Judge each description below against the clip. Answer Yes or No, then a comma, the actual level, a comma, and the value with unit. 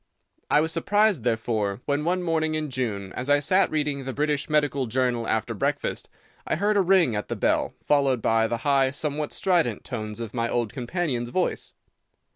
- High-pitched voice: No, medium, 140 Hz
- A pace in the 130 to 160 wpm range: No, average, 185 wpm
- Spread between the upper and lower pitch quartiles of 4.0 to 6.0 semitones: Yes, average, 4.9 semitones